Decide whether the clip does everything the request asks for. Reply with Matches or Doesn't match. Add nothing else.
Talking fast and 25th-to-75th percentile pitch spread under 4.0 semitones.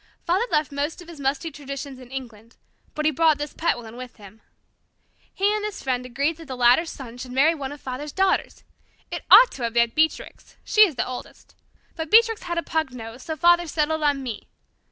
Doesn't match